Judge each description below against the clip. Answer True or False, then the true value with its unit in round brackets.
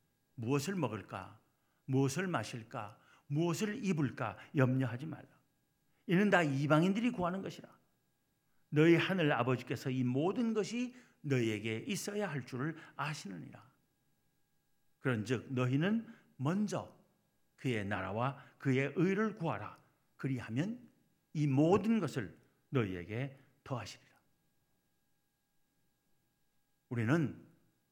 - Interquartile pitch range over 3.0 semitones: True (5.1 semitones)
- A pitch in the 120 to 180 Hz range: True (140 Hz)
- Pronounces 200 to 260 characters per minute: True (230 characters per minute)